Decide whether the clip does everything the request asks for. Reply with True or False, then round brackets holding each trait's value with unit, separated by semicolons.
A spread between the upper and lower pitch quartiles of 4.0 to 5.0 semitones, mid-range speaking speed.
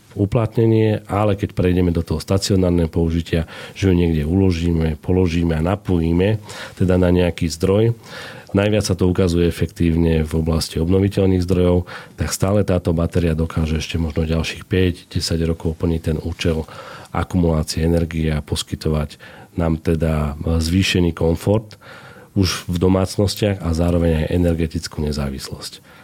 False (2.7 semitones; 130 wpm)